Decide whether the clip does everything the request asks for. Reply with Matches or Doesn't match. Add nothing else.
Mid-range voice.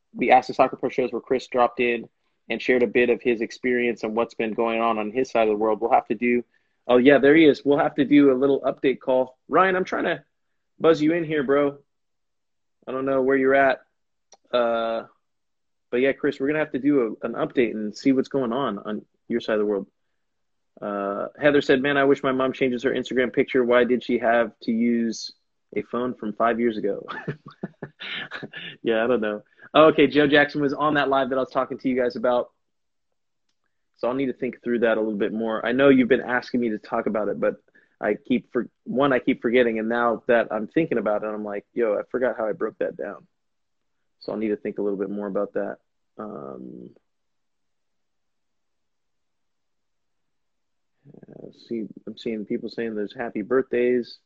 Doesn't match